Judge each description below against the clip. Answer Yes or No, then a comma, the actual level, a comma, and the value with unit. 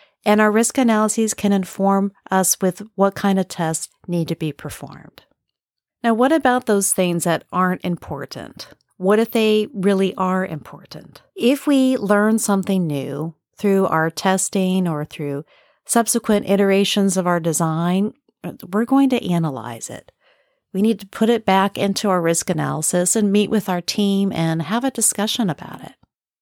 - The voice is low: No, high, 195 Hz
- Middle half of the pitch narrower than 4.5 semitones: Yes, average, 3.4 semitones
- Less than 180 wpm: Yes, average, 160 wpm